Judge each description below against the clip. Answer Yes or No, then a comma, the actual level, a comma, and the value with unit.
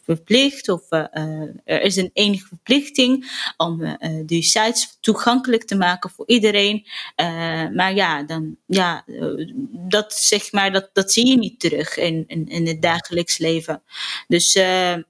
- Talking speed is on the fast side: No, average, 150 wpm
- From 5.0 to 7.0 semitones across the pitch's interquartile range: No, average, 4.4 semitones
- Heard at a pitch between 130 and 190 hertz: Yes, medium, 185 Hz